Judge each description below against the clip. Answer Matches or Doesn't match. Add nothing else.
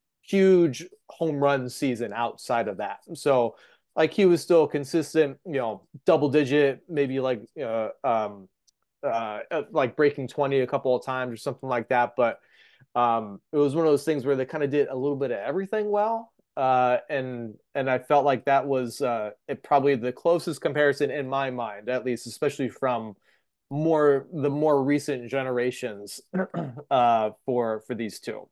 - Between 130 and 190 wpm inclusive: Matches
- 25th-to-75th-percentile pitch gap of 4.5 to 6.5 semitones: Doesn't match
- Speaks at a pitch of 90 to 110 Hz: Doesn't match